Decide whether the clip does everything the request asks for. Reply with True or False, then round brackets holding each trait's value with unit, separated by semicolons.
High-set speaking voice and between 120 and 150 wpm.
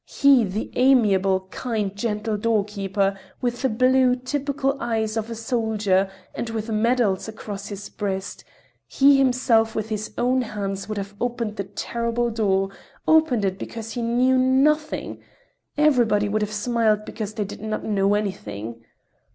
True (220 Hz; 145 wpm)